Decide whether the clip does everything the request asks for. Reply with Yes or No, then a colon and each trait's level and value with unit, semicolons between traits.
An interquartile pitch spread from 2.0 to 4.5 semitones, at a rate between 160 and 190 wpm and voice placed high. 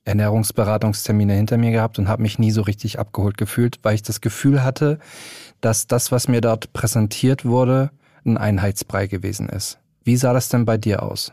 No: average, 2.8 semitones; average, 185 wpm; low, 115 Hz